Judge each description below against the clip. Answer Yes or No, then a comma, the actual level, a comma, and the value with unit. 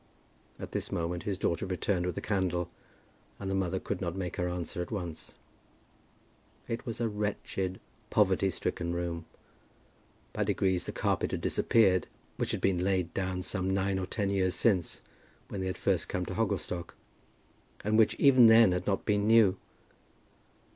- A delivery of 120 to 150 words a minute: No, average, 170 wpm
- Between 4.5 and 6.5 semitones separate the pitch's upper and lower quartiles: No, narrow, 2.4 semitones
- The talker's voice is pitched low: Yes, very low, 95 Hz